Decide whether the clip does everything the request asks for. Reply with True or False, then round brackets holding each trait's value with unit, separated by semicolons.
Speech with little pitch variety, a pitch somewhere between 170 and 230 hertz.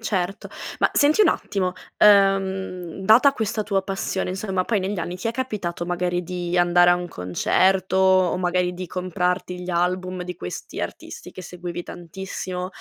True (1.5 semitones; 185 Hz)